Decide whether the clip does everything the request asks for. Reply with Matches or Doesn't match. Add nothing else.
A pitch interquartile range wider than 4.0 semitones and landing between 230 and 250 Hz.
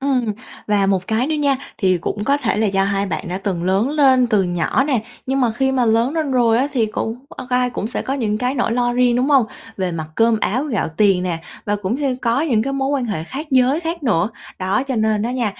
Matches